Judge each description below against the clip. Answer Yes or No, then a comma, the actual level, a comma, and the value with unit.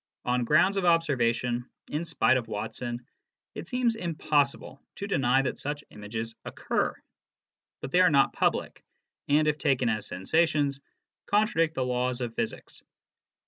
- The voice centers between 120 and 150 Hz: Yes, medium, 140 Hz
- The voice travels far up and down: No, average, 4.9 semitones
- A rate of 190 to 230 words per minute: No, average, 140 wpm